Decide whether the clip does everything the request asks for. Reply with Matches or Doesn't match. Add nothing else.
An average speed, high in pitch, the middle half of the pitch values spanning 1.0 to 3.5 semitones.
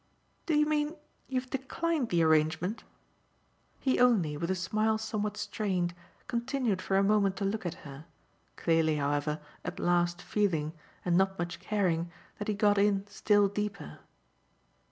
Doesn't match